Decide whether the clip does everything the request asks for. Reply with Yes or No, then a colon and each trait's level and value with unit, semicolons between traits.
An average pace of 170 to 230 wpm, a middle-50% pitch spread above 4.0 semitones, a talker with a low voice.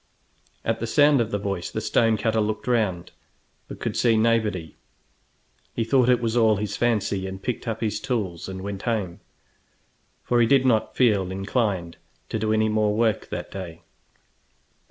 No: average, 175 wpm; average, 3.1 semitones; low, 110 Hz